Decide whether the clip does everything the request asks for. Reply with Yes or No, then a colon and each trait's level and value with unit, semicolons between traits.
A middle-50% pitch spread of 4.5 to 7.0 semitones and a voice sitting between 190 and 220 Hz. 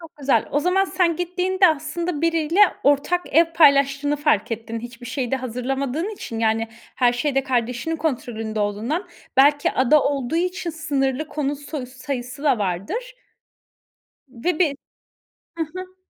No: average, 4.9 semitones; very high, 285 Hz